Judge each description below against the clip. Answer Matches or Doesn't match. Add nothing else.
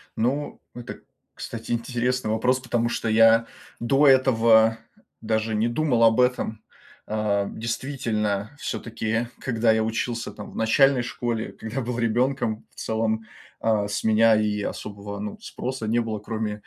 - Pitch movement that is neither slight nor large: Doesn't match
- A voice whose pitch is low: Matches